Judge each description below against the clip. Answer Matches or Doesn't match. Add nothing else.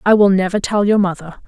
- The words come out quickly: Matches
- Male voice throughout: Doesn't match